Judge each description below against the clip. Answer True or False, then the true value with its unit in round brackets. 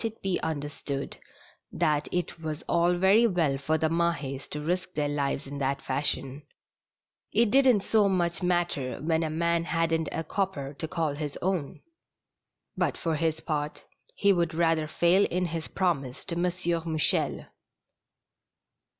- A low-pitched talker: False (165 Hz)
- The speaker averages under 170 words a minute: True (150 wpm)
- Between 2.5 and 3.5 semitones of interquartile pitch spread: True (3.1 semitones)